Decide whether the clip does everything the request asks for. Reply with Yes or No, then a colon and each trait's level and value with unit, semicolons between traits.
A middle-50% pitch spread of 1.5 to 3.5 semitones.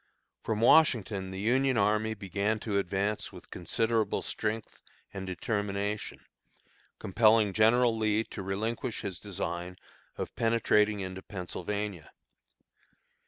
Yes: narrow, 2.4 semitones